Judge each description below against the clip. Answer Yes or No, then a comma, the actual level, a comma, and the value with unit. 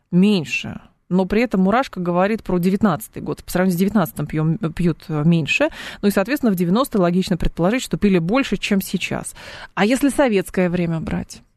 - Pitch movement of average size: Yes, average, 3.6 semitones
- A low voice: No, medium, 185 Hz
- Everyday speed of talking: No, fast, 170 wpm